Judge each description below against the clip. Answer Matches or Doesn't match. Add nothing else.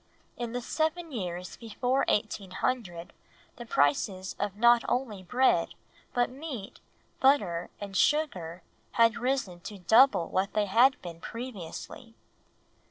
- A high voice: Matches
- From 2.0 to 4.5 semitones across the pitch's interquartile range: Doesn't match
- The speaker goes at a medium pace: Doesn't match